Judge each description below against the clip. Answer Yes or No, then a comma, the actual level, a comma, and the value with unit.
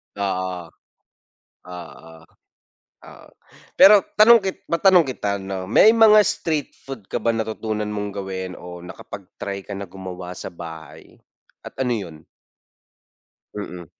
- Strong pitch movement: Yes, wide, 6.6 semitones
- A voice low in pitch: Yes, low, 100 Hz